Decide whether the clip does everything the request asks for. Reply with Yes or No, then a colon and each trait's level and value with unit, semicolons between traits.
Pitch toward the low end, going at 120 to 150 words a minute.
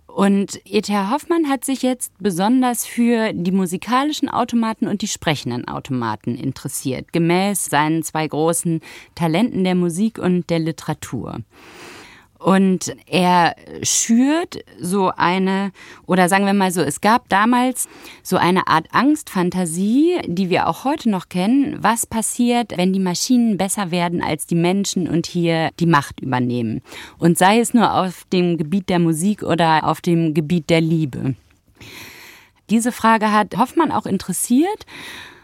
No: medium, 185 Hz; average, 145 wpm